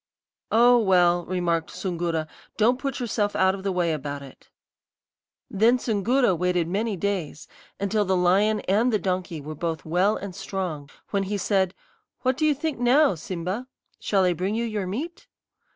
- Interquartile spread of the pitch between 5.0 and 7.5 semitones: No, average, 4.0 semitones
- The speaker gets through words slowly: No, average, 170 wpm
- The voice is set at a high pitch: Yes, high, 195 Hz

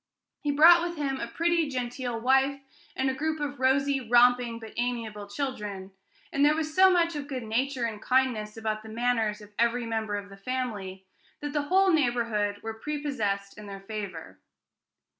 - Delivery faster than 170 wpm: Yes, average, 180 wpm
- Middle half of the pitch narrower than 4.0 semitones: No, average, 4.8 semitones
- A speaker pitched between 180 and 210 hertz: No, high, 245 Hz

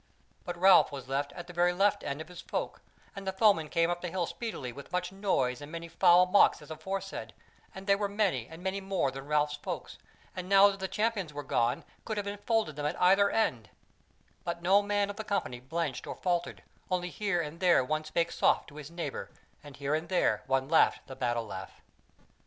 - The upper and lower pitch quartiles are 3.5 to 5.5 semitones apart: Yes, average, 4.8 semitones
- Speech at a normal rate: No, fast, 215 wpm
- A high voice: No, medium, 175 Hz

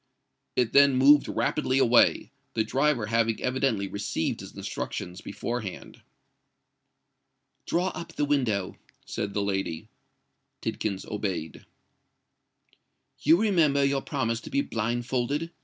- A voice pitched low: Yes, low, 120 Hz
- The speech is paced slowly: Yes, slow, 110 wpm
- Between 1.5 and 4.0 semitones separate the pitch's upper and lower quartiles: No, average, 5.2 semitones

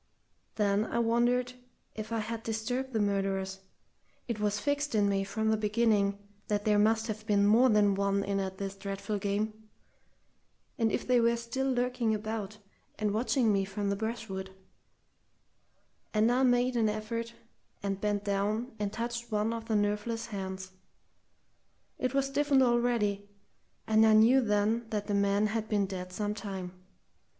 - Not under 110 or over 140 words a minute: No, average, 160 wpm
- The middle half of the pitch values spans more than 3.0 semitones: No, narrow, 2.5 semitones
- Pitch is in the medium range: No, high, 215 Hz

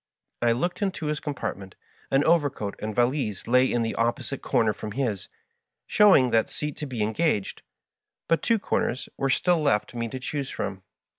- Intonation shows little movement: No, average, 5.1 semitones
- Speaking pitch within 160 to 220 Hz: No, low, 130 Hz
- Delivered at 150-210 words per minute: Yes, average, 170 wpm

